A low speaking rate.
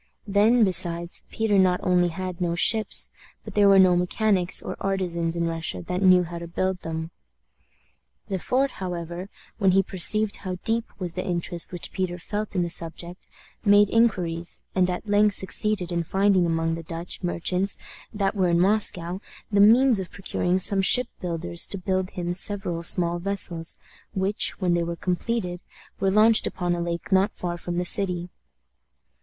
No: average, 170 wpm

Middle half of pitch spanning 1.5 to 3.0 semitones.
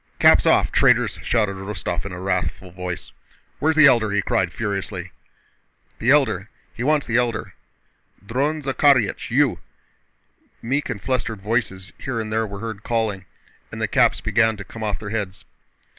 No: average, 4.0 semitones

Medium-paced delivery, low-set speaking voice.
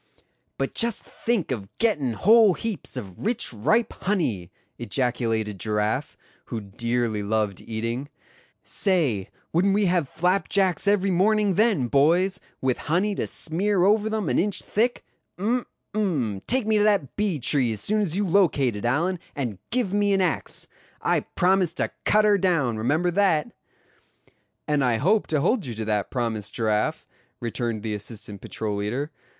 No: average, 160 wpm; medium, 160 Hz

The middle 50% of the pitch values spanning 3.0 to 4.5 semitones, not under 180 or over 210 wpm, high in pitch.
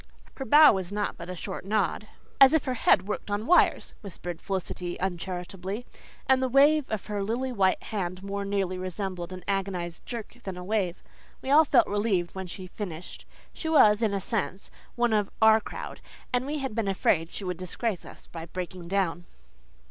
Yes: average, 3.7 semitones; average, 190 wpm; high, 200 Hz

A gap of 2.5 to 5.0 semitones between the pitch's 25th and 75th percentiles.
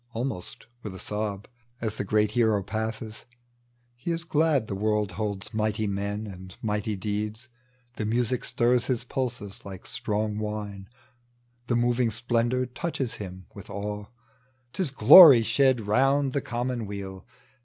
Yes: average, 3.2 semitones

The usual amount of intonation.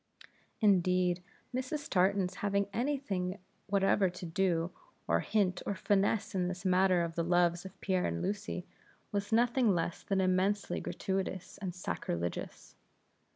No: narrow, 2.2 semitones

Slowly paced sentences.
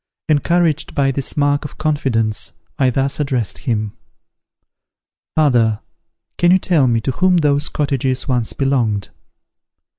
Yes: slow, 125 wpm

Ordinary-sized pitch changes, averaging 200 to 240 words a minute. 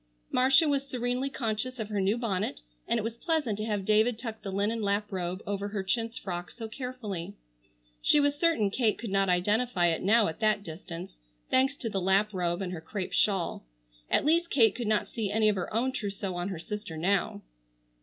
Yes: average, 3.9 semitones; fast, 205 wpm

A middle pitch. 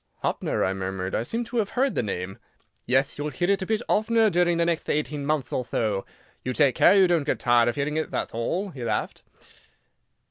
Yes: medium, 150 Hz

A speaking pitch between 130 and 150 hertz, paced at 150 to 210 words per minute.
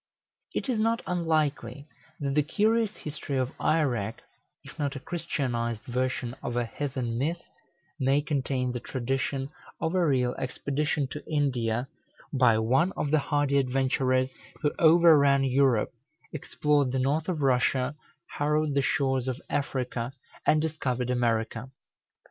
No: low, 135 Hz; slow, 135 wpm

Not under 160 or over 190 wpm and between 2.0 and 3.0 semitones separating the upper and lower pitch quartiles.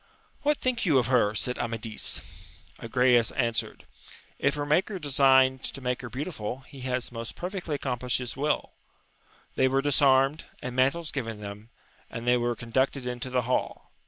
Yes: average, 165 wpm; narrow, 2.6 semitones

